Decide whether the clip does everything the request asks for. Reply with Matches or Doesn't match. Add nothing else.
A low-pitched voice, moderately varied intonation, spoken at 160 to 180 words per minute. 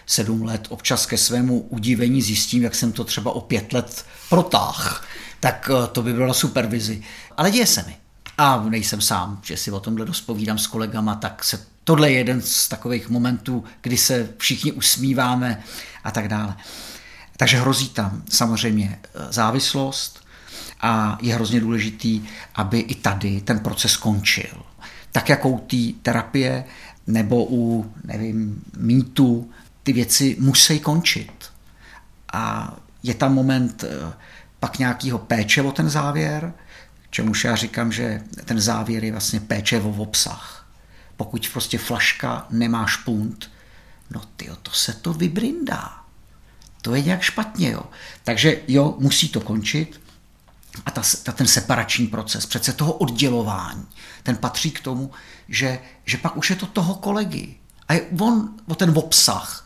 Doesn't match